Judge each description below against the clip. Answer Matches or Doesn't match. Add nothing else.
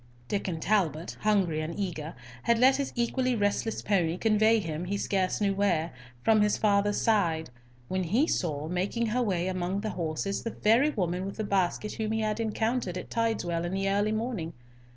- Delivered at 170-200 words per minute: Matches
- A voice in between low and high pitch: Doesn't match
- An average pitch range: Matches